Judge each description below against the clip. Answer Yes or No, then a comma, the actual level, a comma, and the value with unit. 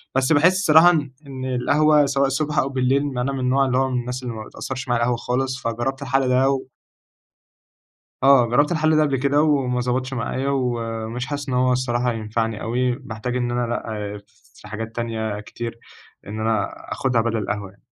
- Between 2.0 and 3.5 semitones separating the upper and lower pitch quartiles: Yes, average, 2.8 semitones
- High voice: No, low, 125 Hz